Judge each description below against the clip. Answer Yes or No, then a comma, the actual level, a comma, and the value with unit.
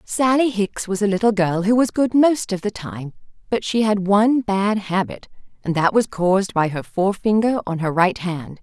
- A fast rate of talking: Yes, fast, 210 wpm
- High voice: Yes, high, 200 Hz